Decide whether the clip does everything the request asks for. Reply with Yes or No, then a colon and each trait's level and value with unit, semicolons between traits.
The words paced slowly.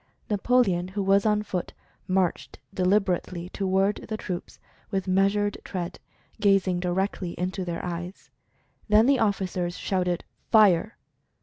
Yes: slow, 130 wpm